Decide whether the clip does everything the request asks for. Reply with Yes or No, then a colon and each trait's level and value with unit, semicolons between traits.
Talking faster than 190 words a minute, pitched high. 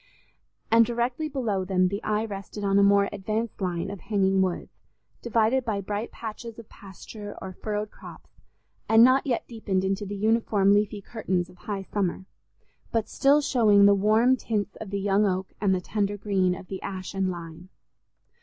No: average, 180 wpm; high, 205 Hz